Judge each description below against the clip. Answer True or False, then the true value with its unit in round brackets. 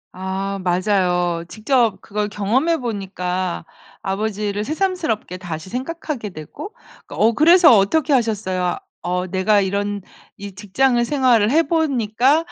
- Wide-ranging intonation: True (5.7 semitones)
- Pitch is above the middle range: True (210 Hz)